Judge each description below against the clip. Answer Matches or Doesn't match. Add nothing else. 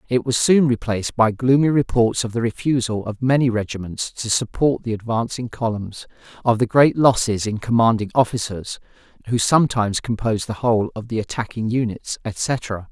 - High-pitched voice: Doesn't match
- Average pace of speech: Matches